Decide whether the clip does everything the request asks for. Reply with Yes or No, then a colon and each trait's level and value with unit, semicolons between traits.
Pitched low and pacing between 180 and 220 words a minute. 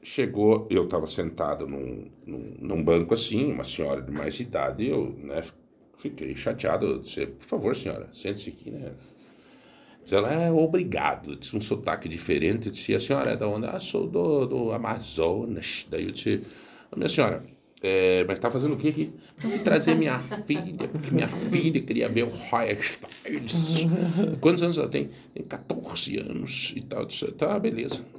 Yes: low, 110 Hz; fast, 185 wpm